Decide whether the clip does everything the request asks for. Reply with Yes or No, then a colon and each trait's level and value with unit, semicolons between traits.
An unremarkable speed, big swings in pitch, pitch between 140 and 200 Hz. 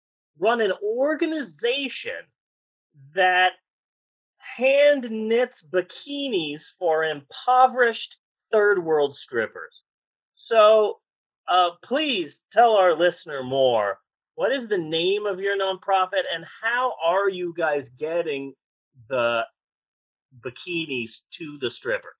No: slow, 100 wpm; wide, 7.4 semitones; high, 190 Hz